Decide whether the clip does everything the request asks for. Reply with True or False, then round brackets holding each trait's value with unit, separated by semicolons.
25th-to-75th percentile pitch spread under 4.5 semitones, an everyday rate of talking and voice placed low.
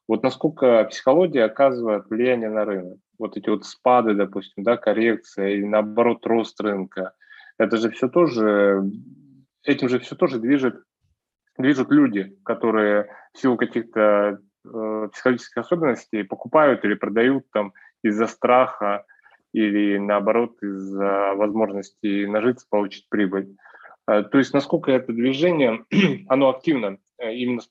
True (3.6 semitones; 130 wpm; 110 Hz)